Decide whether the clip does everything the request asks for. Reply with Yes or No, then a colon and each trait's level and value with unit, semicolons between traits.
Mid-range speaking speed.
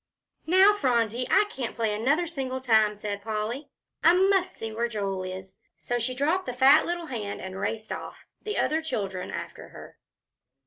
Yes: average, 175 wpm